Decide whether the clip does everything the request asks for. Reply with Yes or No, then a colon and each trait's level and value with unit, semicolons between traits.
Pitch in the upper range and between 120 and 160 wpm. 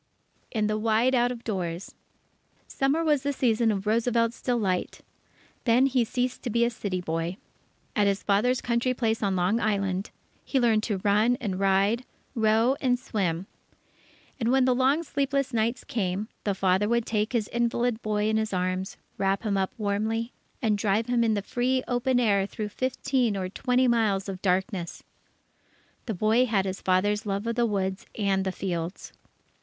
No: high, 220 Hz; average, 175 wpm